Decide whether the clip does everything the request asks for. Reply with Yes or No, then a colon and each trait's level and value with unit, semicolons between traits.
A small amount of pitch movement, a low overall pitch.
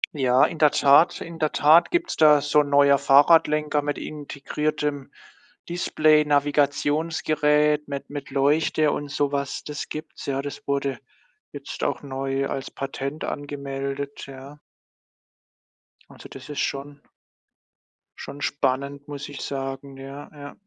No: narrow, 1.4 semitones; medium, 145 Hz